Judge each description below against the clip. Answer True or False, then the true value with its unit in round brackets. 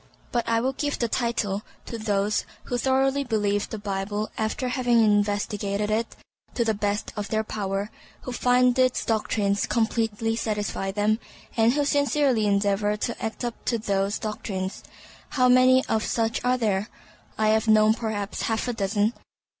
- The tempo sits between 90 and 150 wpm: False (160 wpm)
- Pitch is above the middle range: True (220 Hz)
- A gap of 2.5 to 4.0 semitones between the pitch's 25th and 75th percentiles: True (2.8 semitones)